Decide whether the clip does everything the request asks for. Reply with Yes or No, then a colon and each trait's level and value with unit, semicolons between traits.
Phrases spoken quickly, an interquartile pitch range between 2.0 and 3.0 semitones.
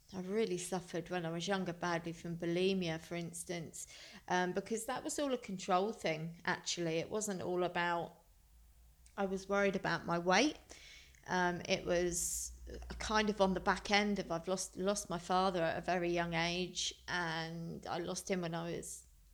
No: average, 180 wpm; narrow, 2.4 semitones